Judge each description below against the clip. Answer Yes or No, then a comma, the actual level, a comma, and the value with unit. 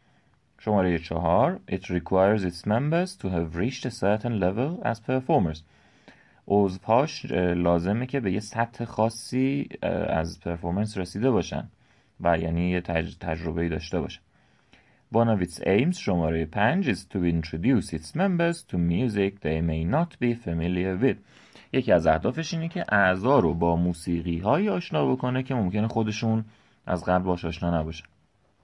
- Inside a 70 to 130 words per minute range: No, average, 150 wpm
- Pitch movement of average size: No, wide, 6.4 semitones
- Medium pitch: No, low, 100 Hz